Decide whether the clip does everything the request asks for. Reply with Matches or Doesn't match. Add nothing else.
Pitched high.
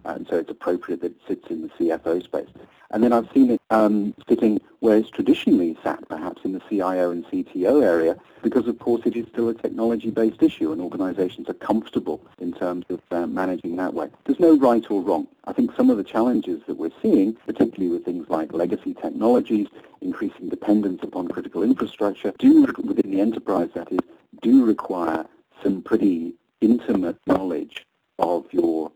Matches